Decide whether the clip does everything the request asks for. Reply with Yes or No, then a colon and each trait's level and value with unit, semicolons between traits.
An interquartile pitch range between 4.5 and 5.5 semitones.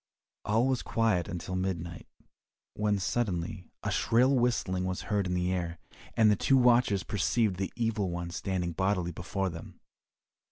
No: average, 4.0 semitones